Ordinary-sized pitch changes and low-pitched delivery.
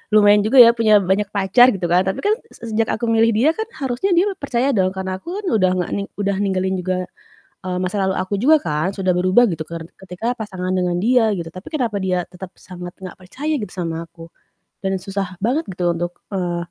No: average, 4.0 semitones; high, 195 Hz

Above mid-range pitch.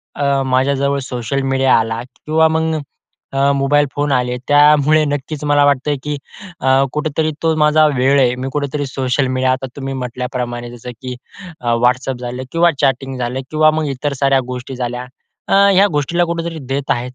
No: low, 135 Hz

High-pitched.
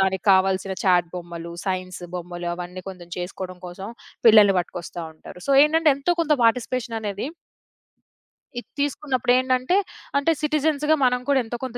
Yes: high, 200 Hz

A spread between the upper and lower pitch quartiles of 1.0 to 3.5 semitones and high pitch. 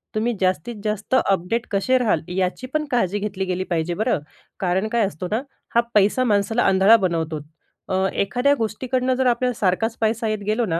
No: average, 4.1 semitones; high, 210 Hz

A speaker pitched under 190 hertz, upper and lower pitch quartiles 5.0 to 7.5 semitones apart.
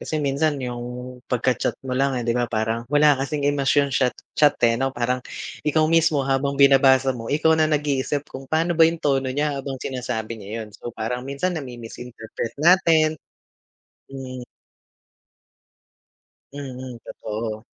No: low, 135 Hz; average, 3.0 semitones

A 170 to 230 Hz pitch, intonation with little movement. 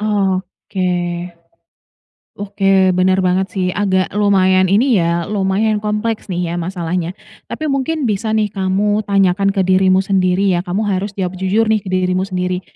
Yes: high, 190 Hz; narrow, 2.1 semitones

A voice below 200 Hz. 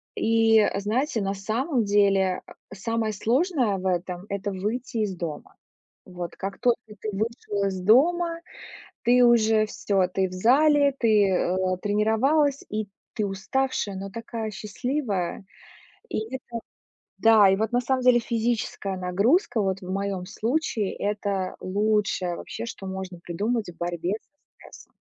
No: high, 210 Hz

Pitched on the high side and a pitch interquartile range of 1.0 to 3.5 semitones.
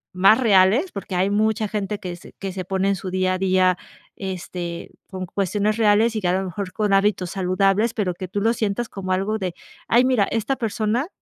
Yes: high, 195 Hz; narrow, 2.6 semitones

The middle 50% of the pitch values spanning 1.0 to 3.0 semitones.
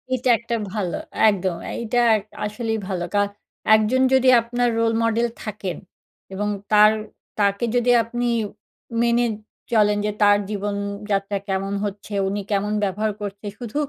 Yes: narrow, 2.6 semitones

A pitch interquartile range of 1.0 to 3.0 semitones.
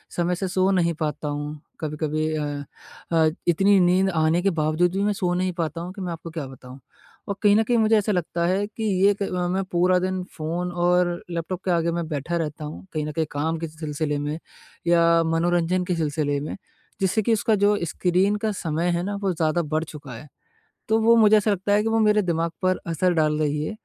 No: average, 3.5 semitones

